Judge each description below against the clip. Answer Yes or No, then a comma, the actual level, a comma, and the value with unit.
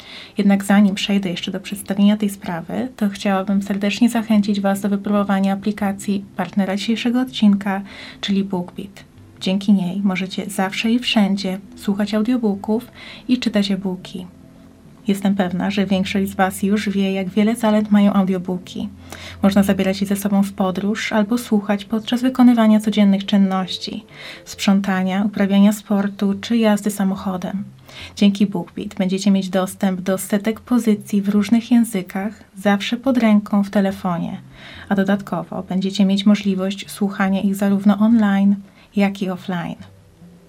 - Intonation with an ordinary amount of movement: No, narrow, 1.4 semitones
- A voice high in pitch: Yes, high, 200 Hz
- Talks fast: No, average, 135 wpm